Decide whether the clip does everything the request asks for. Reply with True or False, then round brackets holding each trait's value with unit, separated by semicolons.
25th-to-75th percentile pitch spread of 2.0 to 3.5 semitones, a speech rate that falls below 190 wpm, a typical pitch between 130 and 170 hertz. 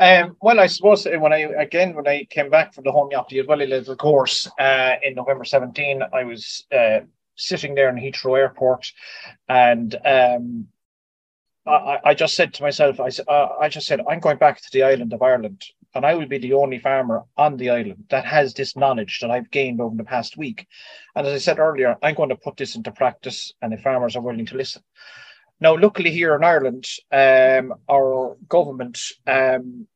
False (3.0 semitones; 200 wpm; 135 Hz)